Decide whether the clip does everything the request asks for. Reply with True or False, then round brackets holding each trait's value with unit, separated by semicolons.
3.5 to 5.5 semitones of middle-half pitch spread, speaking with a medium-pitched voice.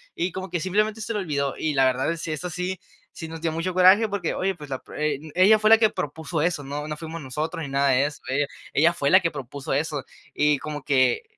True (4.3 semitones; 160 Hz)